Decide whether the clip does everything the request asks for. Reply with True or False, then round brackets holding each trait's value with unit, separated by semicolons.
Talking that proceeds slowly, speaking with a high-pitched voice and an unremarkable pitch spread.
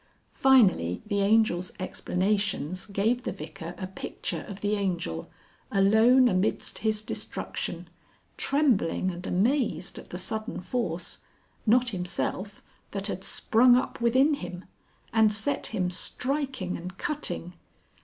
True (125 wpm; 200 Hz; 4.6 semitones)